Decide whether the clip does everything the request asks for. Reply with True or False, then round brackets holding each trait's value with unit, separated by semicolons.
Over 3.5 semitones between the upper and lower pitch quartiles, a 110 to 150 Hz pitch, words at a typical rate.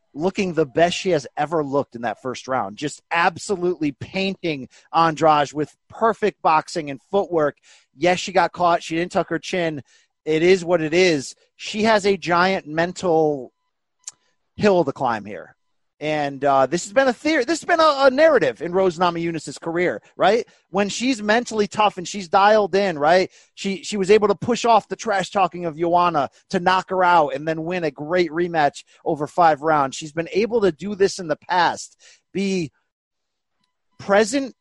False (4.1 semitones; 175 Hz; 185 wpm)